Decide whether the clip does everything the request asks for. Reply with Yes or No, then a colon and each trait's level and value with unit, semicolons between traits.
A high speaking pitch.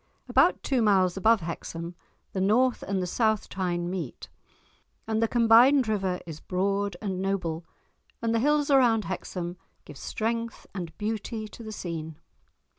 Yes: high, 200 Hz